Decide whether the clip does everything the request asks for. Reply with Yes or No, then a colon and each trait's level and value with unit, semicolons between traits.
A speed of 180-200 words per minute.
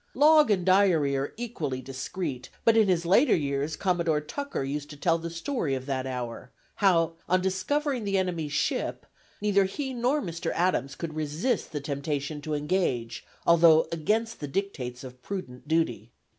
No: average, 165 wpm